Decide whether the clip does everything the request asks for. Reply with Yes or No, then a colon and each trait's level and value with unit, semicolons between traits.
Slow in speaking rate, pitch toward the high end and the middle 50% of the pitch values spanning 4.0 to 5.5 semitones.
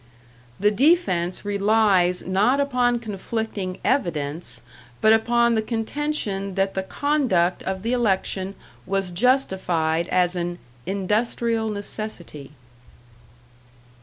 Yes: slow, 100 wpm; high, 205 Hz; average, 4.3 semitones